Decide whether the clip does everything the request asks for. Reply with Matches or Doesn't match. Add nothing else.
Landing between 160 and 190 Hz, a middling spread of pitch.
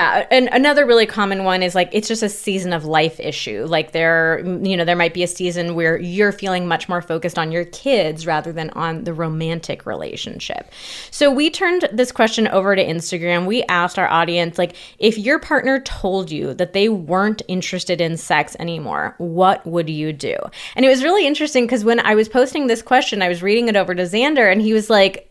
Matches